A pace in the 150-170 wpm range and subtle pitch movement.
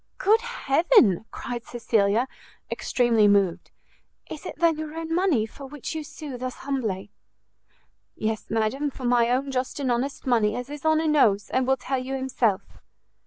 No: average, 165 wpm; average, 4.7 semitones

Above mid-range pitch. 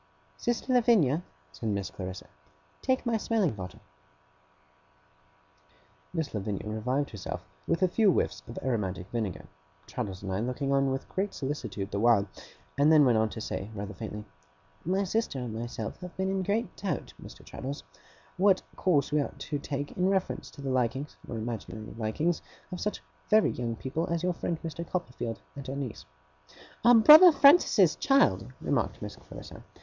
No: medium, 140 Hz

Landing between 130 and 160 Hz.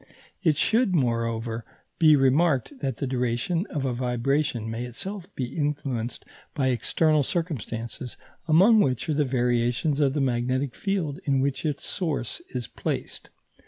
Yes: low, 135 Hz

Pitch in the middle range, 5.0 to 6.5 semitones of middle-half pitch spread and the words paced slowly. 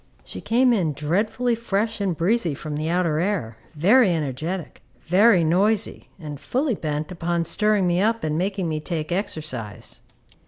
No: medium, 175 Hz; average, 5.3 semitones; average, 155 wpm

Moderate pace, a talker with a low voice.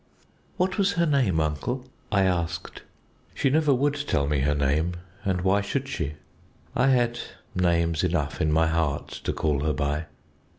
Yes: average, 165 wpm; very low, 90 Hz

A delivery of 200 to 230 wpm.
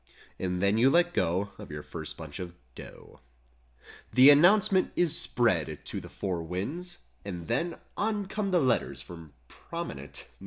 No: average, 155 wpm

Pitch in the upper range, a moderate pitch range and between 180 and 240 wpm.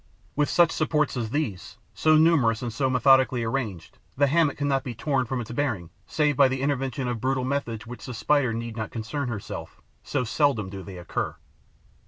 No: low, 130 Hz; average, 4.0 semitones; average, 195 wpm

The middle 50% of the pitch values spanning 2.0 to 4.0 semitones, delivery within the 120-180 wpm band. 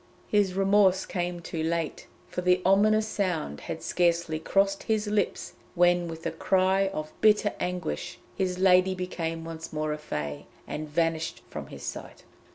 Yes: average, 3.0 semitones; average, 160 wpm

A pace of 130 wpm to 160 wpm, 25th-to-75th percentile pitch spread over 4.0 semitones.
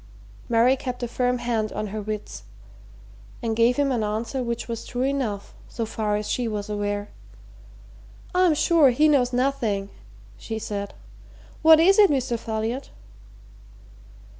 No: average, 145 wpm; average, 3.7 semitones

